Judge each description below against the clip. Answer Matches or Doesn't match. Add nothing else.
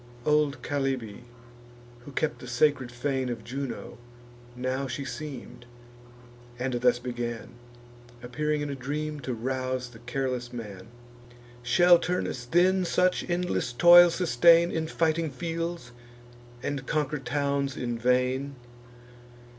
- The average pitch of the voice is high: Doesn't match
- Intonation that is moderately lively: Matches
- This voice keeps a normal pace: Doesn't match